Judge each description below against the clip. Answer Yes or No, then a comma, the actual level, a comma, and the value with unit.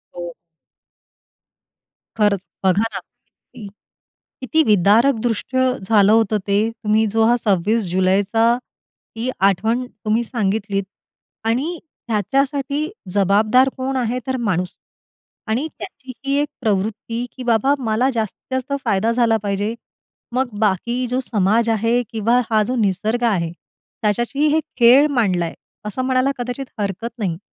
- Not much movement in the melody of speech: No, average, 3.7 semitones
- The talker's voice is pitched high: Yes, high, 225 Hz